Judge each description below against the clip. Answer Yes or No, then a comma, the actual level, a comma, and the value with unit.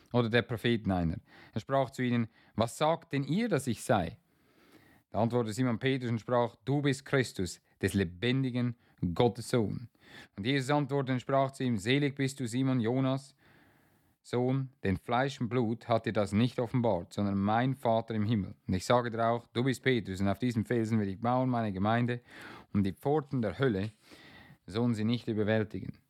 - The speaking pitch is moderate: No, low, 120 Hz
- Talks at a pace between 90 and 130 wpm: No, average, 185 wpm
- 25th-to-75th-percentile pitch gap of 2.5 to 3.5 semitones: Yes, average, 3.1 semitones